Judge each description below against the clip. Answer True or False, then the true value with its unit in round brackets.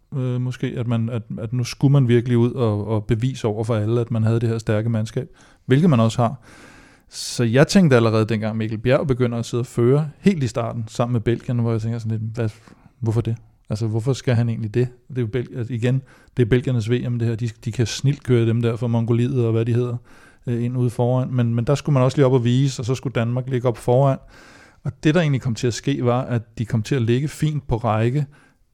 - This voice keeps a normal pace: False (255 wpm)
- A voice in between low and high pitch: False (120 Hz)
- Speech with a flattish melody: True (1.8 semitones)